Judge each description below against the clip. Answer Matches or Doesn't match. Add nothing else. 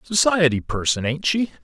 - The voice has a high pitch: Doesn't match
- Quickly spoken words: Doesn't match